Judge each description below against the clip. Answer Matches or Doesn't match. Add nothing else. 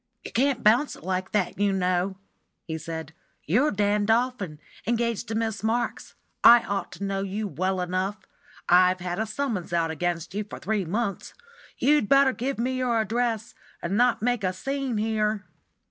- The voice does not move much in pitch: Doesn't match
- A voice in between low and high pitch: Doesn't match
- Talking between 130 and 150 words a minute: Doesn't match